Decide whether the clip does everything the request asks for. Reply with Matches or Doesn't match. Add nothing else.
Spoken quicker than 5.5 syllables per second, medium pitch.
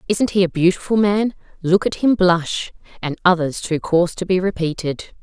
Doesn't match